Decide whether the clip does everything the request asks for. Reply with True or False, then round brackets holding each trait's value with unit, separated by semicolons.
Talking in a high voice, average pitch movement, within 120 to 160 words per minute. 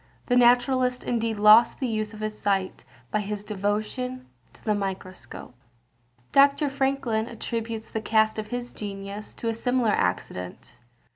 True (220 Hz; 3.0 semitones; 145 wpm)